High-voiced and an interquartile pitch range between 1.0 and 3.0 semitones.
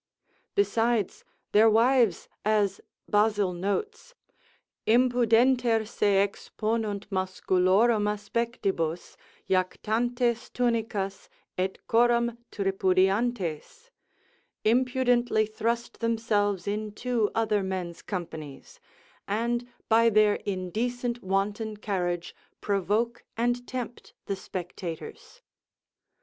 No: high, 215 Hz; average, 3.5 semitones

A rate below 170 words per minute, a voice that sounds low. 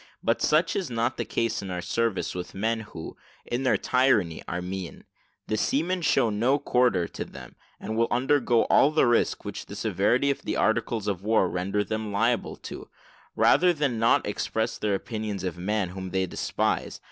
No: average, 190 wpm; low, 110 Hz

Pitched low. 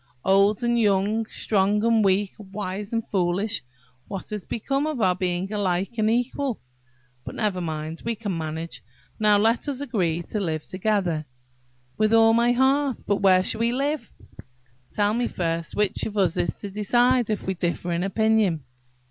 No: high, 205 Hz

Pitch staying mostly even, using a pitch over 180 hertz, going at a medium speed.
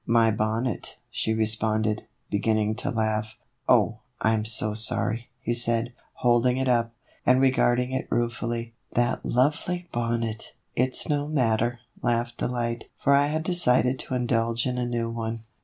No: narrow, 2.0 semitones; low, 120 Hz; average, 165 wpm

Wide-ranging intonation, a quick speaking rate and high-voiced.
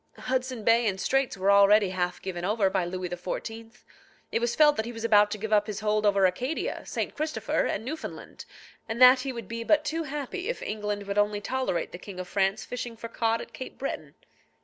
No: average, 4.0 semitones; fast, 215 wpm; high, 220 Hz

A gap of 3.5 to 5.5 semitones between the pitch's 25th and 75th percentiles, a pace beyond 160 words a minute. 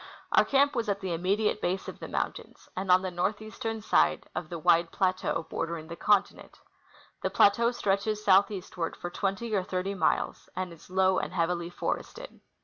No: average, 3.0 semitones; average, 180 wpm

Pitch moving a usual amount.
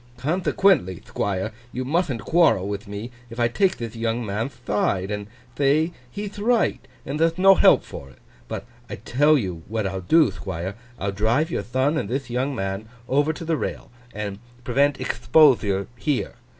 No: wide, 7.2 semitones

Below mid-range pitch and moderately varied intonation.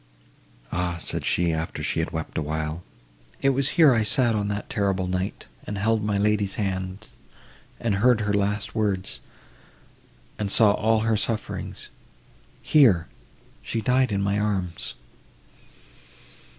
Yes: low, 100 Hz; average, 3.0 semitones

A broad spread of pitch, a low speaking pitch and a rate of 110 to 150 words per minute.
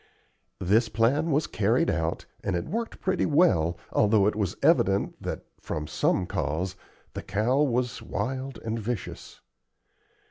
Yes: wide, 6.0 semitones; low, 110 Hz; average, 140 wpm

